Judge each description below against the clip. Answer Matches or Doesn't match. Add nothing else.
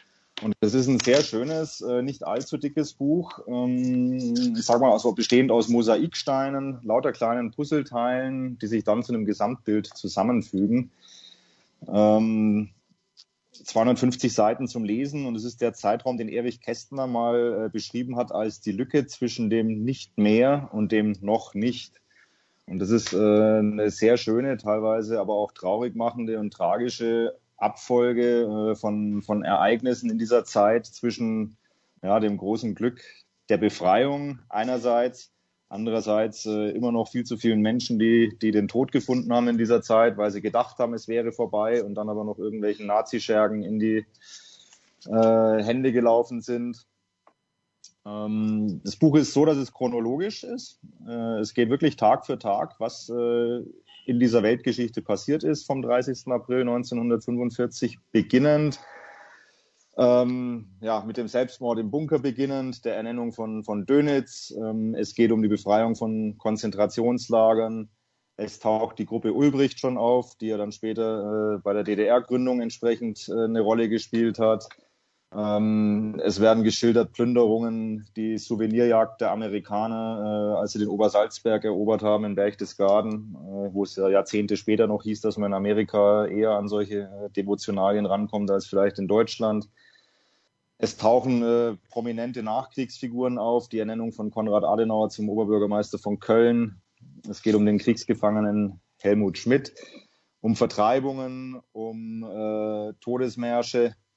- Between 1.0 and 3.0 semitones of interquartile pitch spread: Matches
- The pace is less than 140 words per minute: Doesn't match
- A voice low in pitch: Matches